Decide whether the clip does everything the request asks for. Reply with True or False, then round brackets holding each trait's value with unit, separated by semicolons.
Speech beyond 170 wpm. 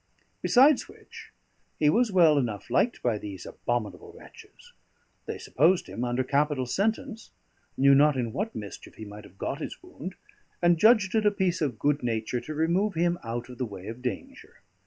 True (180 wpm)